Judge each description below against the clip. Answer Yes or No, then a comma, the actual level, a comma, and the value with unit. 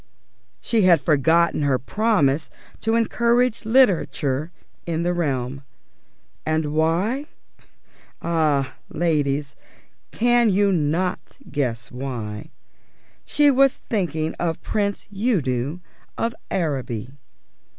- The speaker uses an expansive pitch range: Yes, wide, 7.0 semitones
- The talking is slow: Yes, slow, 95 wpm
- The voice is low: No, medium, 165 Hz